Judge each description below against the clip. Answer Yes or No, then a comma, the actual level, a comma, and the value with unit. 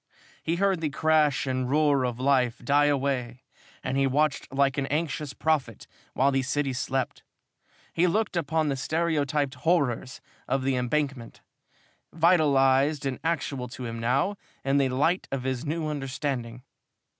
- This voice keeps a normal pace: Yes, average, 150 wpm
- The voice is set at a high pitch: No, medium, 140 Hz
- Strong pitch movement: No, average, 3.0 semitones